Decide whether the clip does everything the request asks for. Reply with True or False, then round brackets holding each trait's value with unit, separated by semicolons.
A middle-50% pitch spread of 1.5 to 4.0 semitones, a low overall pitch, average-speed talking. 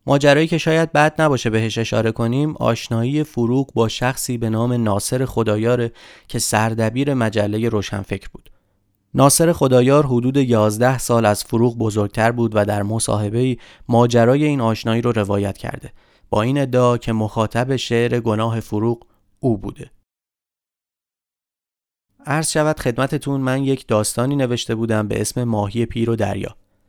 True (3.4 semitones; 115 Hz; 140 wpm)